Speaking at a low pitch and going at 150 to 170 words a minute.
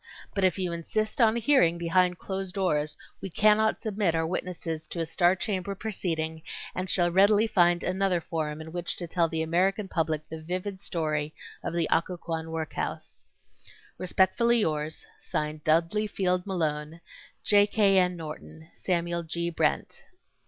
No: medium, 175 Hz; average, 160 wpm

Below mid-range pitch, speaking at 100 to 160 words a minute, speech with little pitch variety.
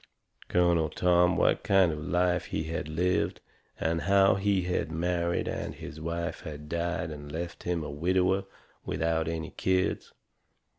Yes: very low, 85 Hz; average, 155 wpm; narrow, 2.0 semitones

